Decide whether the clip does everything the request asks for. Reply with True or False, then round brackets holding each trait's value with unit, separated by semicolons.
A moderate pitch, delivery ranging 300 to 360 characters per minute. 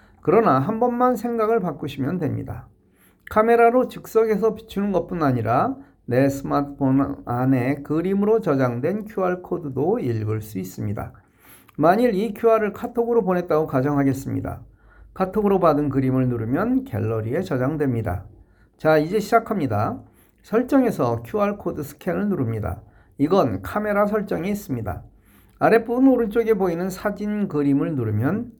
True (155 Hz; 325 characters per minute)